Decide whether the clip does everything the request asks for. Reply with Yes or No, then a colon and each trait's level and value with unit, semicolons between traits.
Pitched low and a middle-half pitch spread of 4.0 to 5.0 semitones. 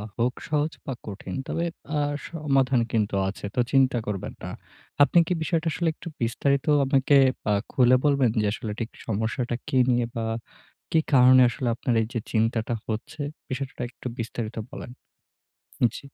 No: low, 125 Hz; average, 3.4 semitones